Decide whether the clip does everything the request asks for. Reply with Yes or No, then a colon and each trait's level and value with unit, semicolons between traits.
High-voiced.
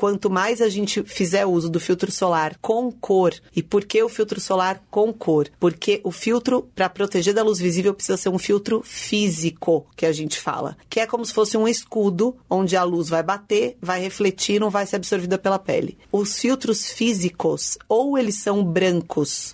Yes: high, 200 Hz